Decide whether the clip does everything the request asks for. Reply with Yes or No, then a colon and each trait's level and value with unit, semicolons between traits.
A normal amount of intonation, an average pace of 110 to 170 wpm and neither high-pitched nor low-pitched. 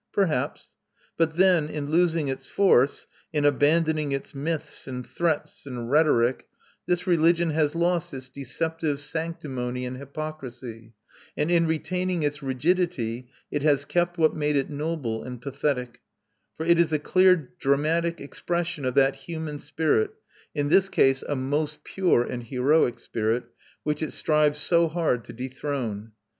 Yes: average, 3.9 semitones; average, 150 wpm; medium, 150 Hz